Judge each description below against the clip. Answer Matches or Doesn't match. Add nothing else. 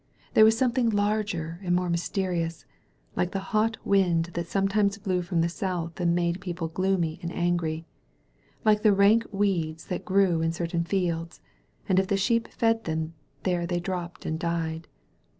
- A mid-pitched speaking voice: Matches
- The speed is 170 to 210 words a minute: Matches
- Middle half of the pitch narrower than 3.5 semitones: Matches